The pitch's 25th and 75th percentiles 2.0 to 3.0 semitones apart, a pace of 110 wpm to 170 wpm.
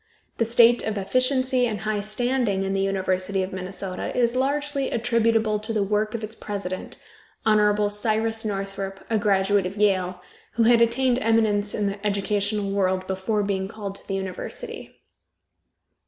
Yes: average, 2.7 semitones; average, 155 wpm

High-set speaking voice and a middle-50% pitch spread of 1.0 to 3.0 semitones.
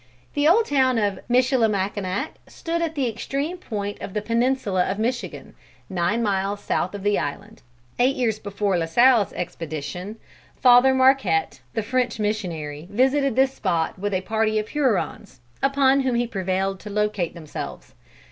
No: high, 215 Hz; average, 5.3 semitones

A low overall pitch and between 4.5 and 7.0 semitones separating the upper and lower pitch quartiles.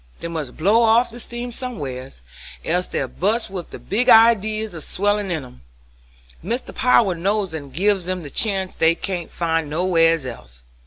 No: medium, 185 Hz; average, 5.0 semitones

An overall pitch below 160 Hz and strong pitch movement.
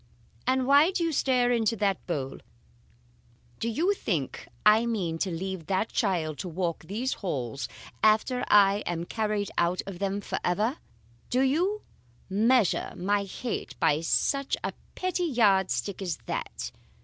No: high, 205 Hz; wide, 5.8 semitones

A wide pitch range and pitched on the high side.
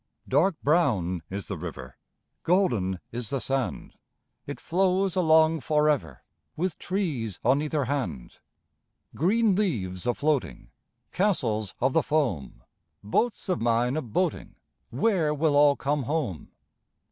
No: wide, 6.6 semitones; medium, 145 Hz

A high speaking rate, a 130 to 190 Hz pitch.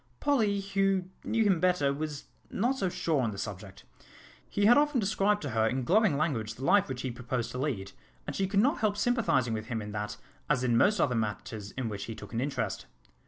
Yes: fast, 220 wpm; medium, 140 Hz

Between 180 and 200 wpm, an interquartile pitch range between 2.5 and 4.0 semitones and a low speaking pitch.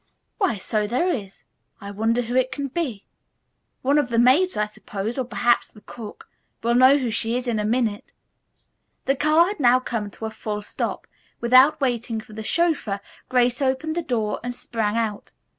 No: average, 190 wpm; average, 3.5 semitones; high, 240 Hz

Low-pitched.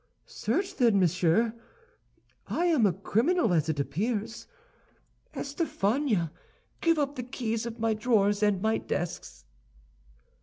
No: high, 220 Hz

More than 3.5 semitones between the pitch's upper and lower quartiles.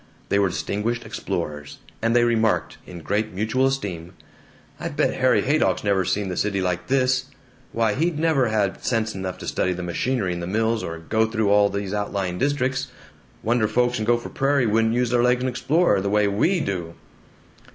Yes: average, 4.2 semitones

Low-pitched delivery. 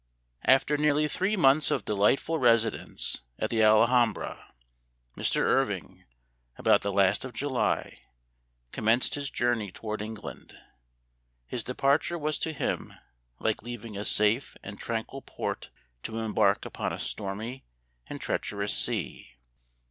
Yes: low, 115 Hz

